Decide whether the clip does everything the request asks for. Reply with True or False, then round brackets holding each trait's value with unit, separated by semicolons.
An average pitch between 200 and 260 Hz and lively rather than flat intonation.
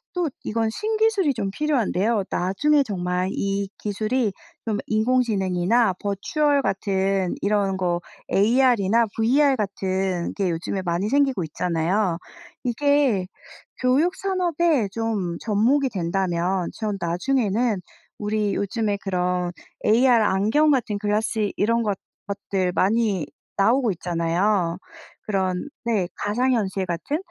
False (210 Hz; 4.6 semitones)